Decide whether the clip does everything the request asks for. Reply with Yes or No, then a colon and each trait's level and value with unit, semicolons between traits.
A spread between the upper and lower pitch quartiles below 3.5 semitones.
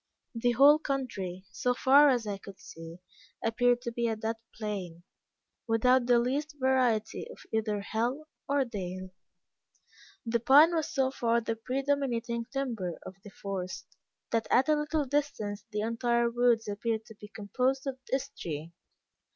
No: average, 4.1 semitones